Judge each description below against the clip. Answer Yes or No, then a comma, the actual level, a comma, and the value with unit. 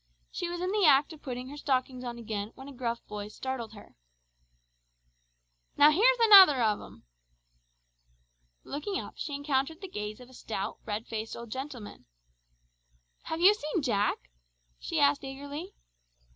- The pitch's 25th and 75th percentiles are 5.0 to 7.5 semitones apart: Yes, wide, 5.5 semitones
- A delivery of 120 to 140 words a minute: No, average, 155 wpm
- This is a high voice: Yes, very high, 265 Hz